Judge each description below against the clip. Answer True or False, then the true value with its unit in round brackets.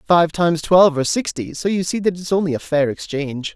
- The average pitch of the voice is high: False (165 Hz)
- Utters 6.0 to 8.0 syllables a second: True (6.5 syllables/s)